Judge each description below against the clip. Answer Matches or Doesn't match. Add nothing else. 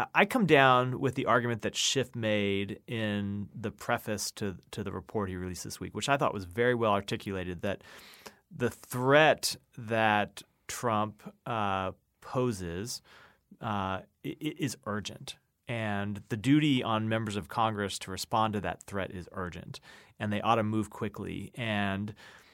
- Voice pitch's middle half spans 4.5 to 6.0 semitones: Doesn't match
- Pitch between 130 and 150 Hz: Doesn't match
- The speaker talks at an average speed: Matches